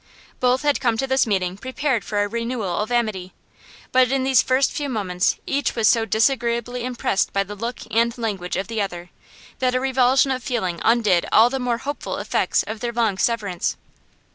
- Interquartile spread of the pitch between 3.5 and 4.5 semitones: Yes, average, 3.8 semitones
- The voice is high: Yes, high, 235 Hz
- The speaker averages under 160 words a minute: No, average, 190 wpm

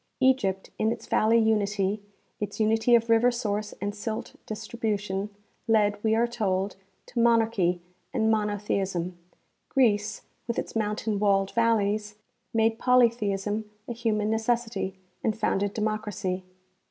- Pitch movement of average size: No, narrow, 2.0 semitones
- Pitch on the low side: No, high, 215 Hz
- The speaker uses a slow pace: Yes, slow, 125 wpm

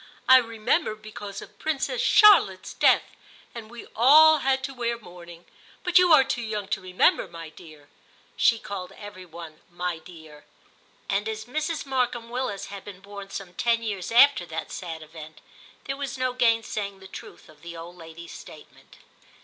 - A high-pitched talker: Yes, high, 205 Hz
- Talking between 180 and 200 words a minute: No, average, 170 wpm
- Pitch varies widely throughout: Yes, wide, 6.2 semitones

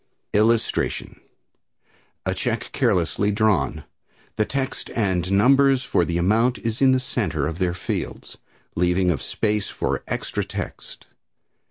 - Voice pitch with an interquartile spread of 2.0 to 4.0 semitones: No, average, 4.9 semitones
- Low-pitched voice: Yes, low, 105 Hz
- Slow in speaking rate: Yes, slow, 130 wpm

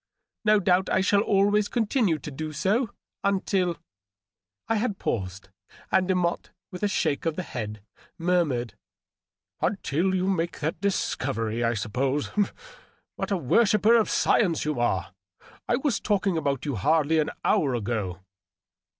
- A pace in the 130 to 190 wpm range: Yes, average, 155 wpm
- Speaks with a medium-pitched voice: Yes, medium, 165 Hz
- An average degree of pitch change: No, wide, 8.1 semitones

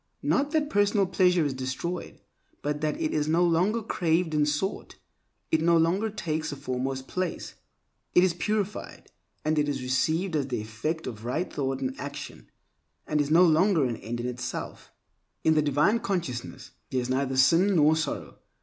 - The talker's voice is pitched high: No, medium, 155 Hz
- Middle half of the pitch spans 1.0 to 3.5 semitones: No, average, 5.2 semitones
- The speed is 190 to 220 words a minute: No, average, 175 wpm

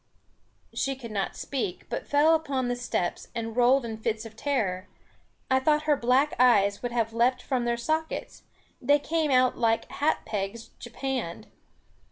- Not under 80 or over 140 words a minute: No, average, 170 wpm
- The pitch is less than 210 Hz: No, high, 245 Hz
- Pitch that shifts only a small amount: No, average, 3.4 semitones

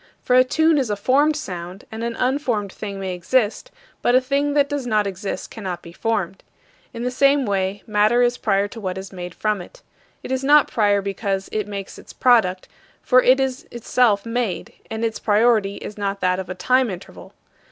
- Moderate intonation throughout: Yes, average, 4.5 semitones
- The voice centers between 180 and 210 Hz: No, high, 220 Hz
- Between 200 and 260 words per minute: Yes, fast, 205 wpm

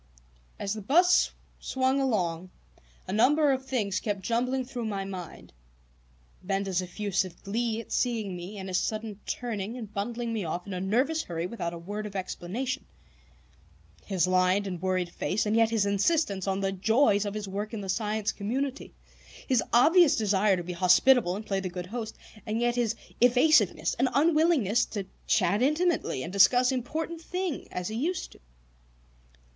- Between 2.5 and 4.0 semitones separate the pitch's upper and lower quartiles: No, average, 4.6 semitones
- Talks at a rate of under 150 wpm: No, average, 170 wpm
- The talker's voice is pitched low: No, high, 215 Hz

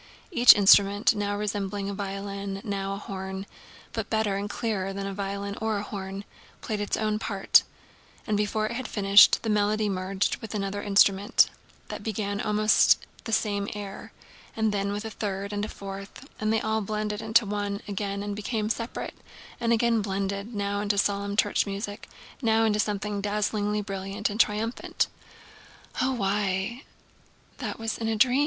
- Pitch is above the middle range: Yes, high, 205 Hz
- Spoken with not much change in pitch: Yes, narrow, 1.4 semitones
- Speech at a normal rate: Yes, average, 160 wpm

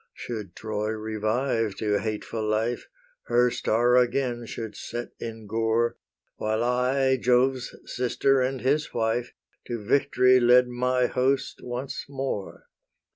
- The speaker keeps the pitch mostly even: Yes, narrow, 2.3 semitones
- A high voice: No, low, 120 Hz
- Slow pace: Yes, slow, 125 wpm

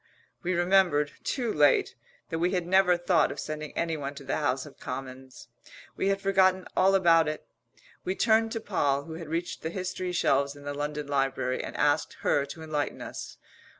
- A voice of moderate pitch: Yes, medium, 165 Hz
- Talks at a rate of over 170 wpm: Yes, average, 185 wpm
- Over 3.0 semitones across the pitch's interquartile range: Yes, average, 4.4 semitones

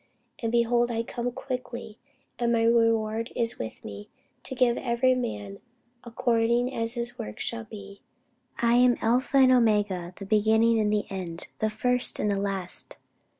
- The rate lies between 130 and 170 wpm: Yes, average, 160 wpm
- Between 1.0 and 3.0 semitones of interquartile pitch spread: Yes, narrow, 2.5 semitones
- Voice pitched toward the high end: Yes, high, 230 Hz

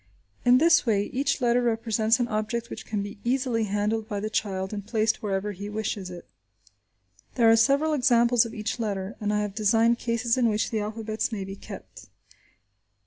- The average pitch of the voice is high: Yes, high, 220 Hz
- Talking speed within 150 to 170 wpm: No, average, 190 wpm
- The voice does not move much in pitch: Yes, narrow, 2.3 semitones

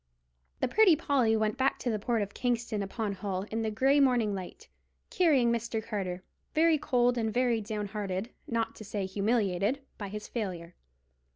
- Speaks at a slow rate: No, average, 165 wpm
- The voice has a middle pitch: No, high, 220 Hz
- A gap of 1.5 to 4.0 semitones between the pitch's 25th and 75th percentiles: Yes, average, 3.4 semitones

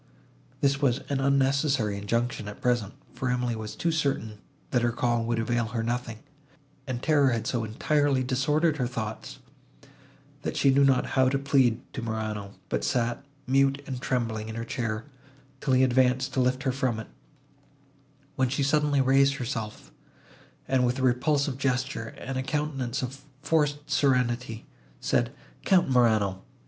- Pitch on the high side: No, low, 130 Hz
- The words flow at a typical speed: Yes, average, 160 wpm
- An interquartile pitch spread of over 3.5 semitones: No, average, 2.9 semitones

